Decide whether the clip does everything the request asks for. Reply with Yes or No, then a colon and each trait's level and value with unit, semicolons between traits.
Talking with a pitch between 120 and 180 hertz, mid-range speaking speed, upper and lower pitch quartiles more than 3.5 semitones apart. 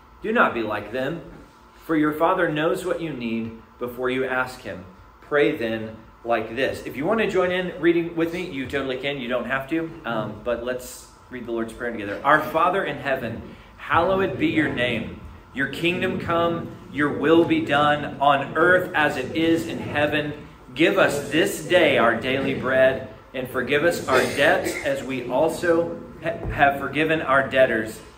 Yes: low, 135 Hz; average, 180 wpm; average, 5.3 semitones